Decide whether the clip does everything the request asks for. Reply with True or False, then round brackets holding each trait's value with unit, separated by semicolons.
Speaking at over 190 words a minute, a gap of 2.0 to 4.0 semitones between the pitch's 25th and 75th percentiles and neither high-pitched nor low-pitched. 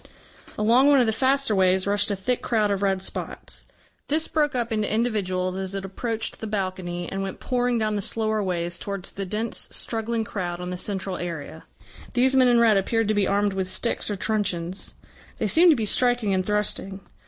False (200 wpm; 3.5 semitones; 205 Hz)